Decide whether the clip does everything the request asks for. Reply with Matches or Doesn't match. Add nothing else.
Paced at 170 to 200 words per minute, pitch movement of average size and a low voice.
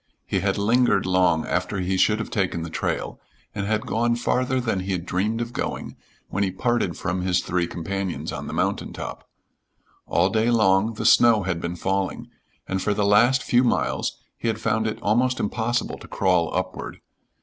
Matches